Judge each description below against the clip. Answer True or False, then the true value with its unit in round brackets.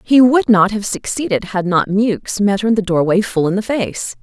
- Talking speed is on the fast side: True (240 wpm)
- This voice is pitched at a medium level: False (205 Hz)